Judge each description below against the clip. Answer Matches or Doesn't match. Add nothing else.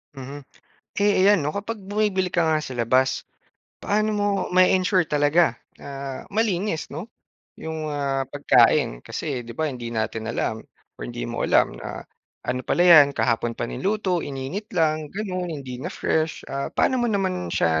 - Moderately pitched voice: Matches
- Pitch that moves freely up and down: Matches